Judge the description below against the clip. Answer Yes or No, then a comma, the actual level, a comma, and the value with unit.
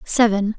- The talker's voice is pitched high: Yes, high, 215 Hz